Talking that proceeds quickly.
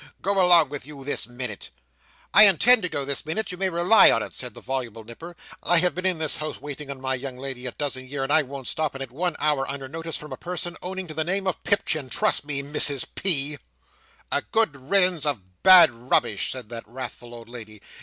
Yes: fast, 230 wpm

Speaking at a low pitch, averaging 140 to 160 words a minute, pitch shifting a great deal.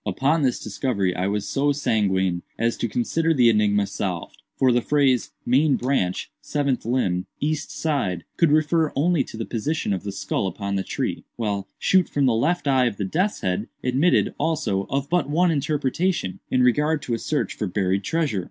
No: low, 125 Hz; average, 190 wpm; wide, 6.8 semitones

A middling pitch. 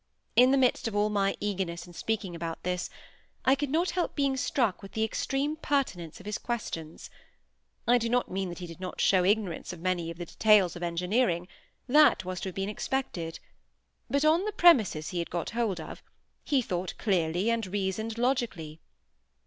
No: high, 200 Hz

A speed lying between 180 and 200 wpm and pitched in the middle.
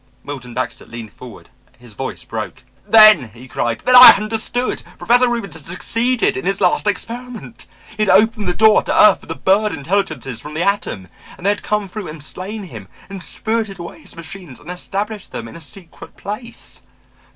No: average, 190 wpm; high, 195 Hz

